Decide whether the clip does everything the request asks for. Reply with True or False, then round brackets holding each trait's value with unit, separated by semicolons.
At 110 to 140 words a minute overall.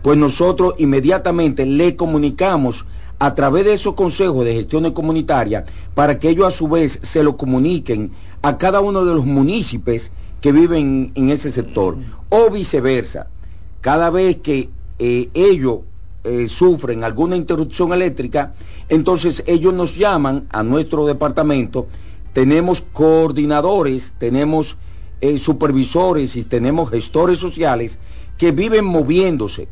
True (130 wpm)